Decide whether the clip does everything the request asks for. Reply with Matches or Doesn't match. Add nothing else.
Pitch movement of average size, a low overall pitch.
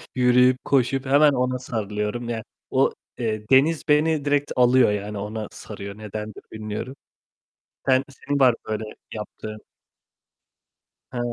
Matches